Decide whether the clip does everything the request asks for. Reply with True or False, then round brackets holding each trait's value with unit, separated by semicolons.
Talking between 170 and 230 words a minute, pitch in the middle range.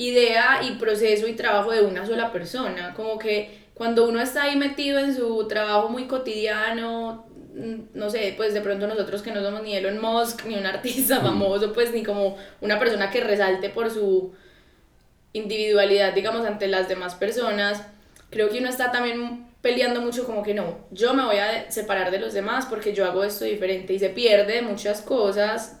False (185 wpm; 215 Hz)